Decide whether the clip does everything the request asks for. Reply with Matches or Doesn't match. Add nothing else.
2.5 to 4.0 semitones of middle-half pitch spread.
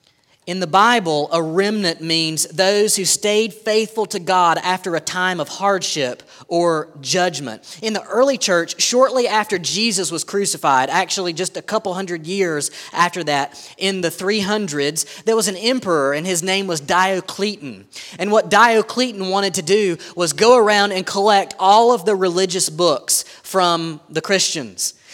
Matches